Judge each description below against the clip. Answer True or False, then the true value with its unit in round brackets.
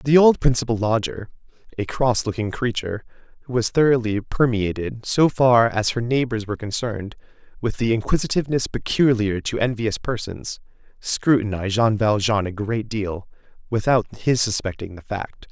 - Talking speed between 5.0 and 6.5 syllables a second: True (5.1 syllables/s)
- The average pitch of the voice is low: True (115 Hz)